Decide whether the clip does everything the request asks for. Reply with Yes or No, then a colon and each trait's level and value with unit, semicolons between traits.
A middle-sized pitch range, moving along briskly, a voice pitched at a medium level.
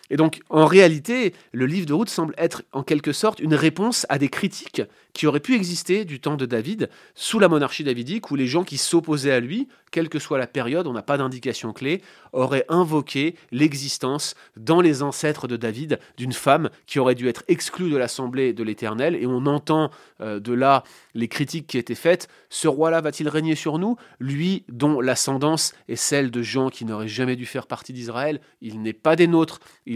No: average, 4.3 semitones; average, 205 wpm; medium, 145 Hz